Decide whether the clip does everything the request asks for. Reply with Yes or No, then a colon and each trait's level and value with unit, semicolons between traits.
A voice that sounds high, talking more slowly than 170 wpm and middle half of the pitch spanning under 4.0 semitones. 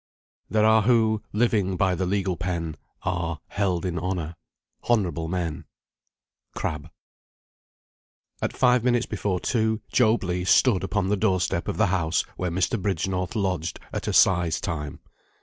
No: very low, 95 Hz; average, 145 wpm; average, 3.6 semitones